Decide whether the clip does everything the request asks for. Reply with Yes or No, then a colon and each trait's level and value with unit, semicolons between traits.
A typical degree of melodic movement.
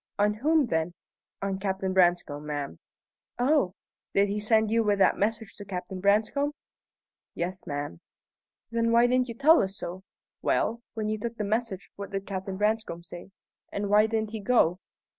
Yes: average, 3.2 semitones